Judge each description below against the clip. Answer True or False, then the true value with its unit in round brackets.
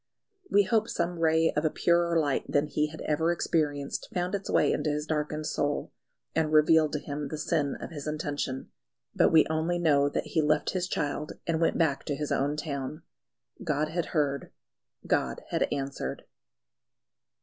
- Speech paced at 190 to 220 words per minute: False (175 wpm)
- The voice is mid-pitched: True (155 Hz)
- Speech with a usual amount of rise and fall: False (1.9 semitones)